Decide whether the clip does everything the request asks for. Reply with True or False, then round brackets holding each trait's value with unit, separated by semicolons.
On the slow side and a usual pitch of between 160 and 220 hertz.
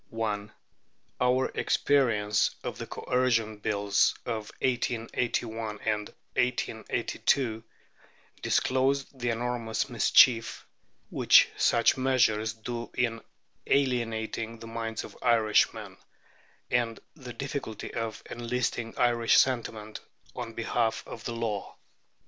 False (95 wpm; 115 Hz)